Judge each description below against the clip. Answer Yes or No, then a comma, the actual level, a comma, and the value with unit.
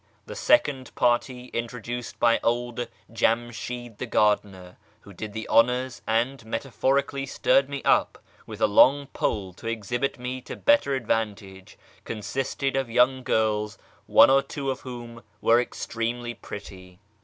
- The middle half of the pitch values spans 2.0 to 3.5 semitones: Yes, average, 2.9 semitones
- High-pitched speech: No, low, 120 Hz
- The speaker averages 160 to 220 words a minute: No, average, 145 wpm